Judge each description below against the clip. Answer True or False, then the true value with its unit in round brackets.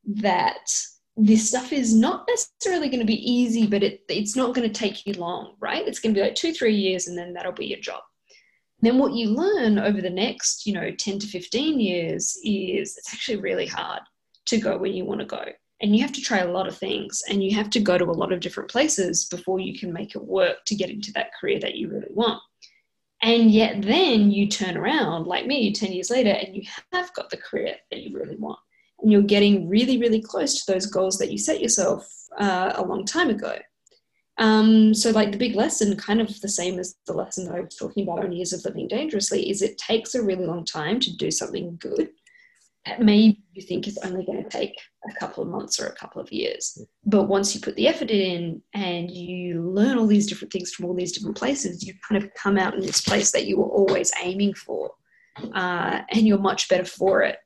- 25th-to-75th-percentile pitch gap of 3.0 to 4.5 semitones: True (3.7 semitones)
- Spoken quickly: True (235 wpm)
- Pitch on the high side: True (205 Hz)